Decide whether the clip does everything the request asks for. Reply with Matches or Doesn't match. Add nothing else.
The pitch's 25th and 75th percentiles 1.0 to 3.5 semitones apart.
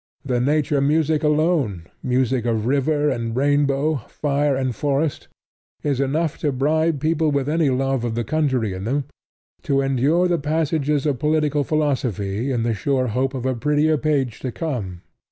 Matches